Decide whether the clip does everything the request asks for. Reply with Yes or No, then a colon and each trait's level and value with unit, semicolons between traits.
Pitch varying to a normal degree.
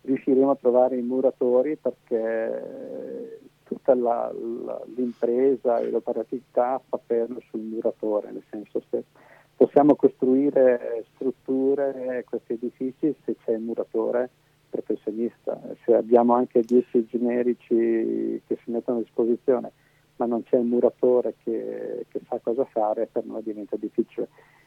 No: narrow, 2.0 semitones